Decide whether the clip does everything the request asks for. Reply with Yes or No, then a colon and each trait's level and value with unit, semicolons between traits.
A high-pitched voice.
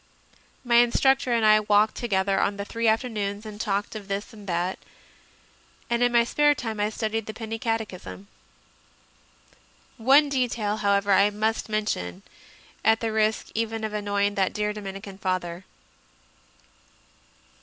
Yes: high, 215 Hz